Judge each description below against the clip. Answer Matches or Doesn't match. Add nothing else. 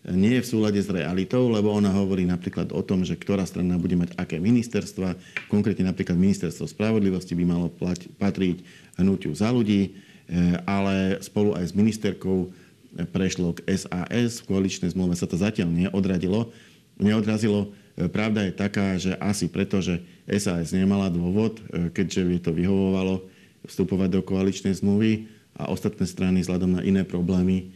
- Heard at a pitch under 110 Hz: Matches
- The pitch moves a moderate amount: Doesn't match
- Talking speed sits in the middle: Matches